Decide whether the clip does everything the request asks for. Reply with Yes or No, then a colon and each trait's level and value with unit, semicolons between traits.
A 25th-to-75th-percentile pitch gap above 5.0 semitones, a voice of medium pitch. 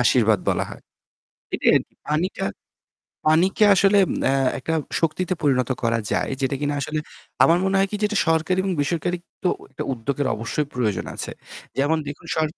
Yes: wide, 5.6 semitones; medium, 155 Hz